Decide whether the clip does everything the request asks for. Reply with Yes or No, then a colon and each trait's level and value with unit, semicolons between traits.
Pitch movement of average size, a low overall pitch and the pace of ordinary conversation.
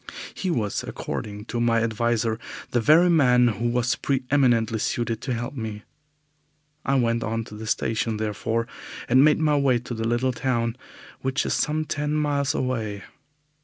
Yes: average, 3.2 semitones; low, 120 Hz; average, 165 wpm